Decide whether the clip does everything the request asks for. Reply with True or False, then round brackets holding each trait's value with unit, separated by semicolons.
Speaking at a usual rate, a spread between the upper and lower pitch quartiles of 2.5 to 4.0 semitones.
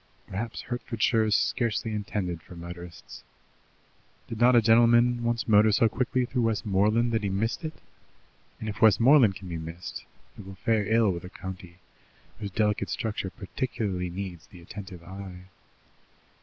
True (155 wpm; 3.6 semitones)